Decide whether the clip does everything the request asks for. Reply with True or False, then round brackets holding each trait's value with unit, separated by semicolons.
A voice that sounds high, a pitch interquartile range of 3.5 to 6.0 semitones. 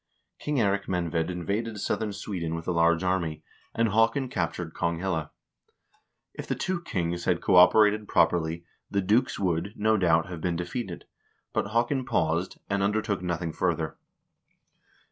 False (90 Hz; 4.1 semitones)